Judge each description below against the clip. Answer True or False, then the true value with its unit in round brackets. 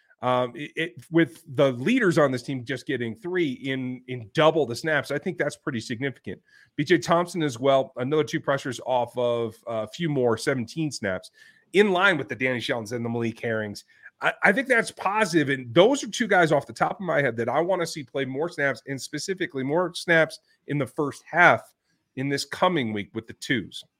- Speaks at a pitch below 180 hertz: True (140 Hz)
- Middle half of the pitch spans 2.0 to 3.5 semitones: False (4.7 semitones)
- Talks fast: True (215 wpm)